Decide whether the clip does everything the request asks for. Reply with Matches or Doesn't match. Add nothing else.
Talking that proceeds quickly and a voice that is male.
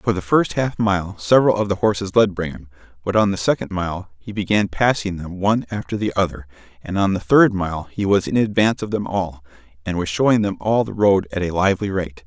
Matches